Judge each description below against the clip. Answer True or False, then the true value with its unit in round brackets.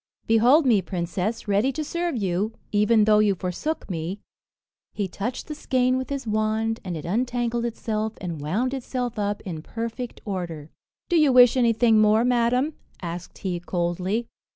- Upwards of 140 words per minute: True (160 wpm)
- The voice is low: False (220 Hz)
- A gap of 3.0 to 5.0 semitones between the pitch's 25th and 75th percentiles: True (4.7 semitones)